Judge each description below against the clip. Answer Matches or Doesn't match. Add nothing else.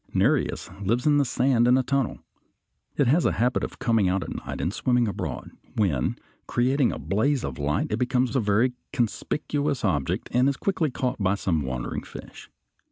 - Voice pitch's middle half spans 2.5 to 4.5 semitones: Doesn't match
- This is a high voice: Doesn't match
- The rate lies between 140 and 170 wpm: Doesn't match